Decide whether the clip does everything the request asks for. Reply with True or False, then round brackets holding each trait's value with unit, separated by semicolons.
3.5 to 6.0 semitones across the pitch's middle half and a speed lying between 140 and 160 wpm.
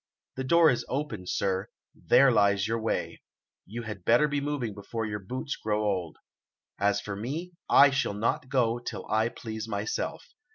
False (4.2 semitones; 170 wpm)